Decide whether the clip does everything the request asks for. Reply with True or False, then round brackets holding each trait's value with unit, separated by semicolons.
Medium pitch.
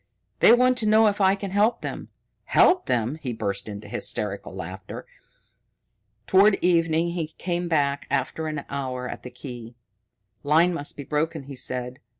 True (155 Hz)